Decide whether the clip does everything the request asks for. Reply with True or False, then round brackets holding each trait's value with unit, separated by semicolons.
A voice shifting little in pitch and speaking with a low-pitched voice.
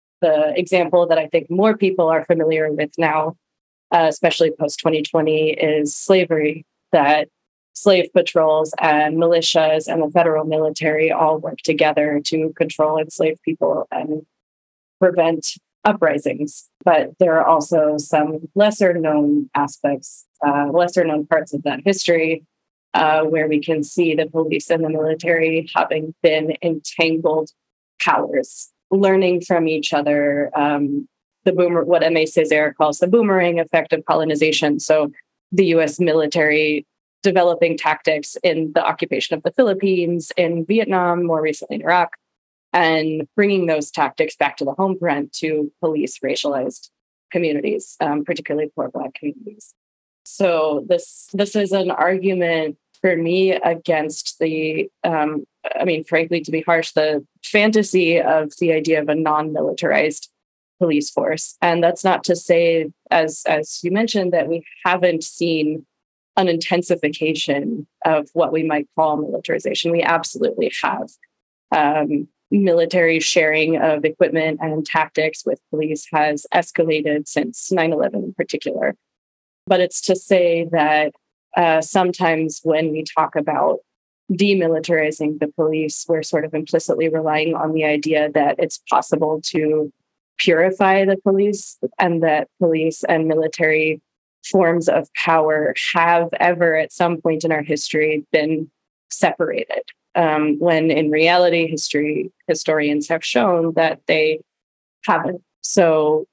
False (2.1 semitones; 160 Hz)